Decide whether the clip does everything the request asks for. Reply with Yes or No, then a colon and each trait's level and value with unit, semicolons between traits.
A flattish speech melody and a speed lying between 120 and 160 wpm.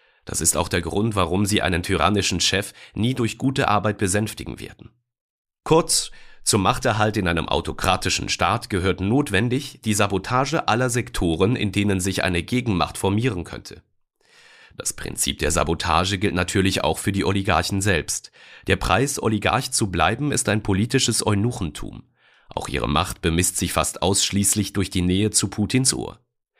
No: average, 3.7 semitones; average, 155 wpm